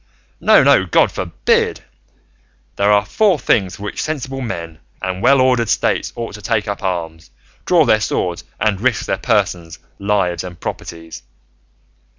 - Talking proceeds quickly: No, average, 155 wpm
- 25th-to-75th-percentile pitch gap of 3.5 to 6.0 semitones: Yes, average, 4.9 semitones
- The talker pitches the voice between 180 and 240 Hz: No, low, 100 Hz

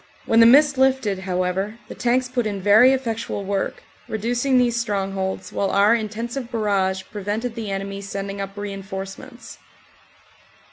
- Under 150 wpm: Yes, average, 140 wpm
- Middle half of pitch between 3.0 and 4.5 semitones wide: Yes, average, 3.3 semitones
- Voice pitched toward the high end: Yes, high, 210 Hz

